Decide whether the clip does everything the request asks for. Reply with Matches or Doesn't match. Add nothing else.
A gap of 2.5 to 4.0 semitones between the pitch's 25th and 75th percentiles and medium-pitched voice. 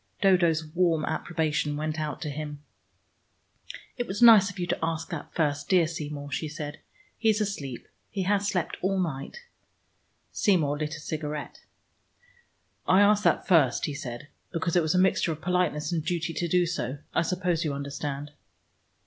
Matches